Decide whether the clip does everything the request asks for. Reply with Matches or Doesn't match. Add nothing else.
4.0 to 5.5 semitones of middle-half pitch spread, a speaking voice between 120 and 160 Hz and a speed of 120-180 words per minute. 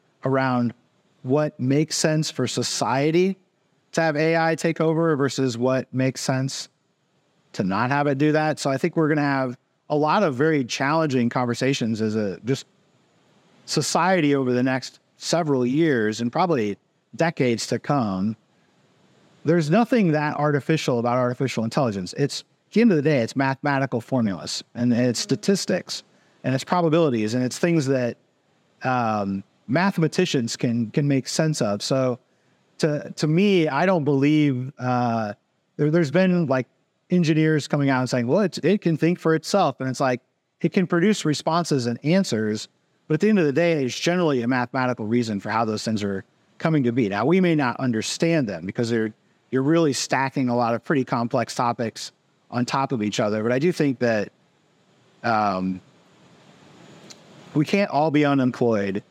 Matches